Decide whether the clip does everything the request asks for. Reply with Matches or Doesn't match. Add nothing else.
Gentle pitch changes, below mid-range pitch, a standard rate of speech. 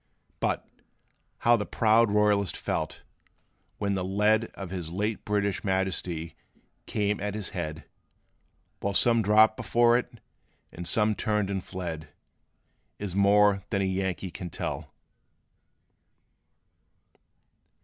Doesn't match